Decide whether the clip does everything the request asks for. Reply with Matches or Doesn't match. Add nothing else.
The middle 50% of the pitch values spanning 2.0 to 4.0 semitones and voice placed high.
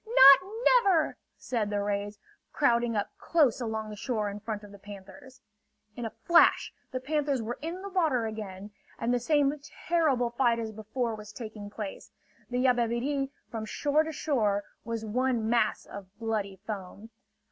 Doesn't match